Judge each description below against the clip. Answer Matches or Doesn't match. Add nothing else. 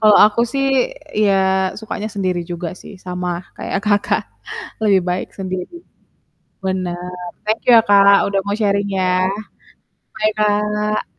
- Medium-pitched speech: Doesn't match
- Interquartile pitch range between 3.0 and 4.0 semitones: Doesn't match